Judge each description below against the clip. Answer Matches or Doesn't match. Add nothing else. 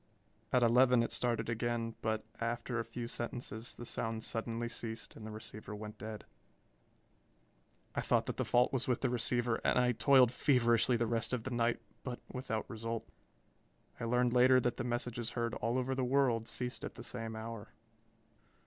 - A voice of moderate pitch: Doesn't match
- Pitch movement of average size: Doesn't match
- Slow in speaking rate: Doesn't match